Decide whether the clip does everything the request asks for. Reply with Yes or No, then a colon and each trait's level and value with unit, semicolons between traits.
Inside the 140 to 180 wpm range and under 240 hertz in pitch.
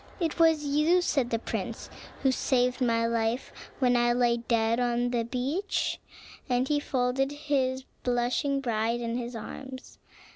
No: average, 150 wpm; very high, 250 Hz